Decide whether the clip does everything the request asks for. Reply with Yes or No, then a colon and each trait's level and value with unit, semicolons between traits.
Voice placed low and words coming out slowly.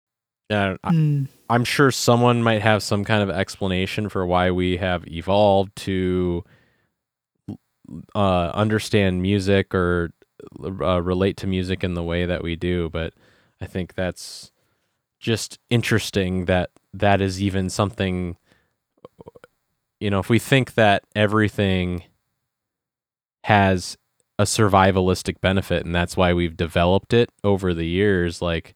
Yes: very low, 95 Hz; slow, 130 wpm